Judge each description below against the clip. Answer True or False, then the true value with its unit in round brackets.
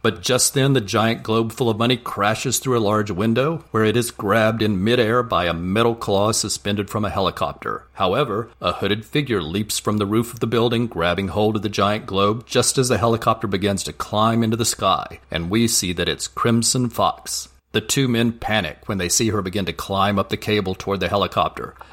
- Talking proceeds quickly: True (215 wpm)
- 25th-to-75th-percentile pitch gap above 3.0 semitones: False (2.7 semitones)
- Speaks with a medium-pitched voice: False (110 Hz)